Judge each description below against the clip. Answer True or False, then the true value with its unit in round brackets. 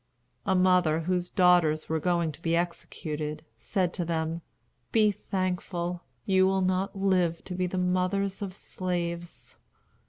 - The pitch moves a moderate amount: False (1.8 semitones)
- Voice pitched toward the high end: False (180 Hz)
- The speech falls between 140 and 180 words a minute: True (145 wpm)